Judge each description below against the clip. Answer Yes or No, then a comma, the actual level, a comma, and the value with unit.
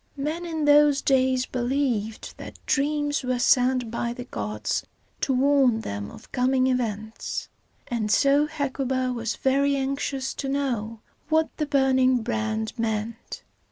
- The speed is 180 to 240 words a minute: No, slow, 135 wpm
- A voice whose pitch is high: Yes, very high, 255 Hz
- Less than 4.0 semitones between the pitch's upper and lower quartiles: Yes, average, 3.4 semitones